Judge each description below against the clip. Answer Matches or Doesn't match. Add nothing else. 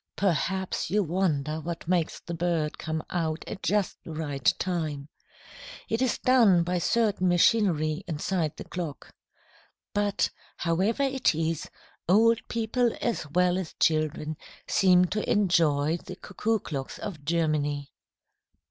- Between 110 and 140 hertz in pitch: Doesn't match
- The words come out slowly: Matches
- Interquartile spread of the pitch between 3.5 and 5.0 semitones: Matches